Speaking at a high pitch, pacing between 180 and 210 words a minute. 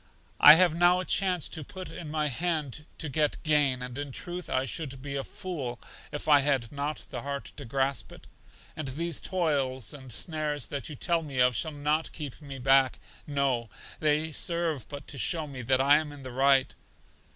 No: medium, 145 Hz; average, 195 wpm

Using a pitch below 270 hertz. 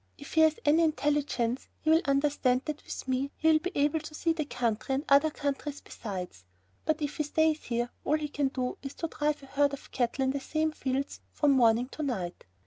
No: very high, 285 Hz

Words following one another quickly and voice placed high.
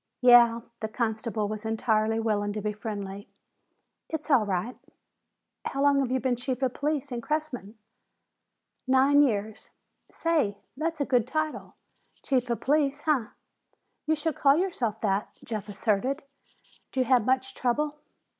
No: average, 145 wpm; very high, 250 Hz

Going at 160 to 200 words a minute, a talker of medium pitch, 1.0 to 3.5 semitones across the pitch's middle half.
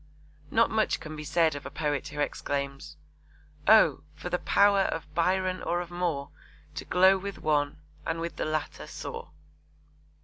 No: average, 165 wpm; medium, 165 Hz; average, 3.9 semitones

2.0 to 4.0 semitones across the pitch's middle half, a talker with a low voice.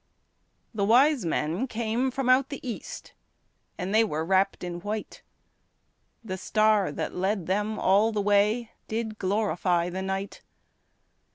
No: average, 3.0 semitones; high, 210 Hz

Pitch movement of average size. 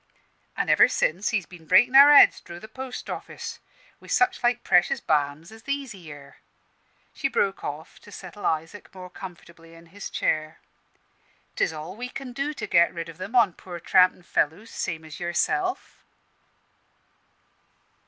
No: wide, 5.9 semitones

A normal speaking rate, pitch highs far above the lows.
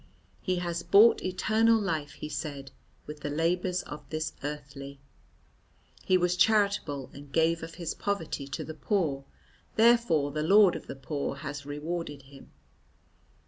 No: average, 145 wpm; average, 4.1 semitones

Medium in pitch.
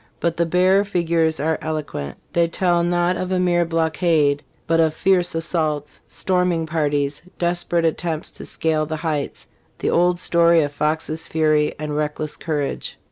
Yes: medium, 165 Hz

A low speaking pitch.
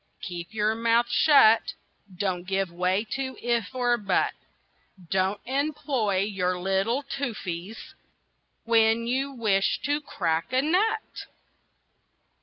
No: high, 220 Hz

